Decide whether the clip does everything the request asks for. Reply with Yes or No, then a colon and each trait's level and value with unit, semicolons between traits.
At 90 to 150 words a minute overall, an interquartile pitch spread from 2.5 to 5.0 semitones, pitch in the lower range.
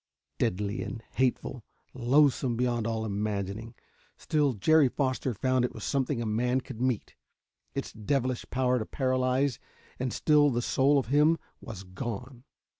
Yes: average, 145 wpm; average, 2.9 semitones; low, 125 Hz